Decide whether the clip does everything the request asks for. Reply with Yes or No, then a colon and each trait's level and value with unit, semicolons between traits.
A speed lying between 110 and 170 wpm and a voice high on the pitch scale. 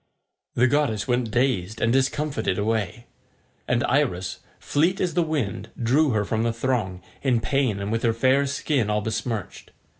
No: average, 160 wpm; low, 115 Hz